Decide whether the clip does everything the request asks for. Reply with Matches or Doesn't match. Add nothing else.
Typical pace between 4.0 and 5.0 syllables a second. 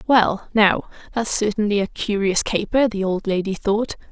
Matches